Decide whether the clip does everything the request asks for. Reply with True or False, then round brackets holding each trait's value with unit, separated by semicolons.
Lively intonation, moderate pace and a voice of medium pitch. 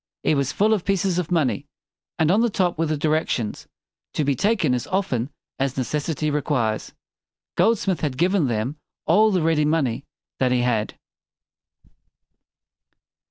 True (5.7 semitones; 170 wpm; 155 Hz)